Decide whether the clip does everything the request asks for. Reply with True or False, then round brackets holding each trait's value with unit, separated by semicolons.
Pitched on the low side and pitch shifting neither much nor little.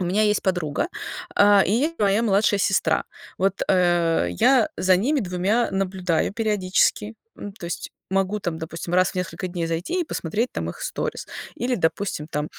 False (190 Hz; 3.2 semitones)